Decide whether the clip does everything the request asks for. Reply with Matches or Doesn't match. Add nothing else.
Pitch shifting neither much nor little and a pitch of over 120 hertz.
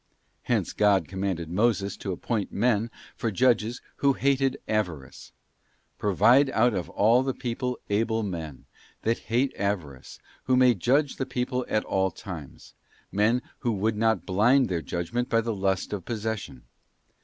Doesn't match